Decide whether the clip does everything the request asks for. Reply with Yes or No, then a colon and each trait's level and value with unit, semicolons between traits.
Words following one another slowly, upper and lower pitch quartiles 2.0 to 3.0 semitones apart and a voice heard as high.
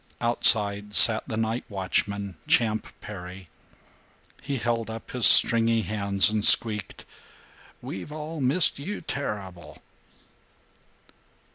No: slow, 105 wpm; average, 2.7 semitones; low, 110 Hz